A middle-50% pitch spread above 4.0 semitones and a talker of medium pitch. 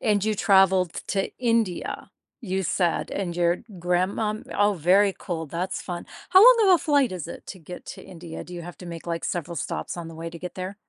No: average, 3.0 semitones; medium, 180 Hz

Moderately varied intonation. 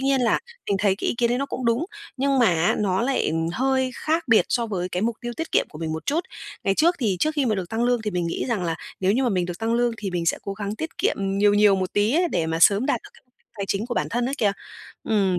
Yes: average, 4.7 semitones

